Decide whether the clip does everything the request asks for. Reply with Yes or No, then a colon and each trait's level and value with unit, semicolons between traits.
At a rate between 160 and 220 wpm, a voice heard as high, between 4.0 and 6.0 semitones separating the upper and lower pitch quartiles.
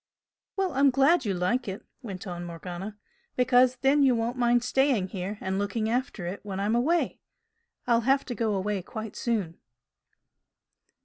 Yes: average, 165 wpm; high, 230 Hz; average, 4.8 semitones